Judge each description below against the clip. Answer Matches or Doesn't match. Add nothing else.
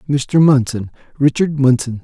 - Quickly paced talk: Doesn't match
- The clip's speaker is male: Matches